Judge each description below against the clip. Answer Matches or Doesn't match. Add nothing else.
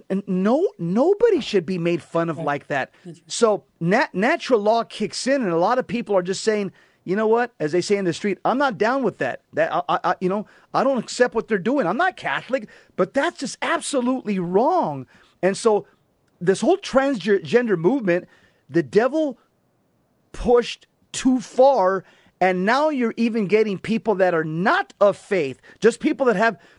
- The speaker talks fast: Doesn't match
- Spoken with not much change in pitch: Doesn't match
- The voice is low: Doesn't match